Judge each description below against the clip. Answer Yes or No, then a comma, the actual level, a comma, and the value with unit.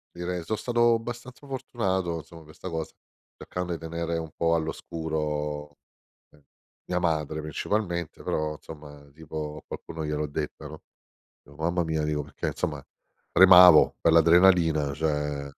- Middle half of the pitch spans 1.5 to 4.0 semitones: Yes, average, 2.7 semitones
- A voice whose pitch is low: Yes, very low, 80 Hz